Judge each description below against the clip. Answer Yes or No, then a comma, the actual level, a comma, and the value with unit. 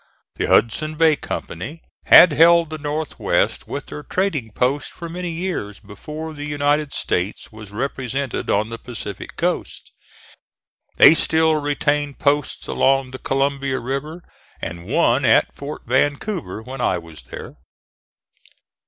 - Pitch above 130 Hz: Yes, medium, 140 Hz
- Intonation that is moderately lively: Yes, average, 5.0 semitones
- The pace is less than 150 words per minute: Yes, slow, 135 wpm